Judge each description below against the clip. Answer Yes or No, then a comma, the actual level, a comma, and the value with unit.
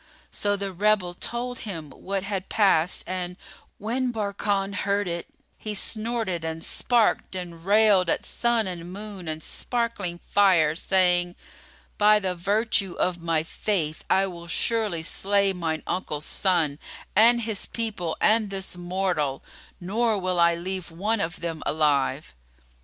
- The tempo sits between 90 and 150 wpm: Yes, average, 140 wpm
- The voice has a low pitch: No, high, 190 Hz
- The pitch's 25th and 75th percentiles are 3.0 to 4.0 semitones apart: Yes, average, 3.6 semitones